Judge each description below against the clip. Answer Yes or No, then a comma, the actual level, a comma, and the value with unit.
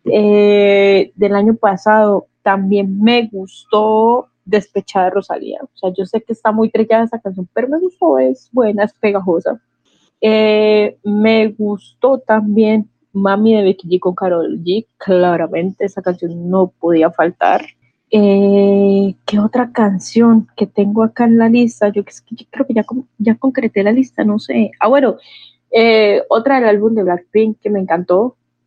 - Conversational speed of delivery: Yes, average, 155 wpm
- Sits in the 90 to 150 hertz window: No, high, 210 Hz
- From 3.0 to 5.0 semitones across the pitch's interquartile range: No, narrow, 2.5 semitones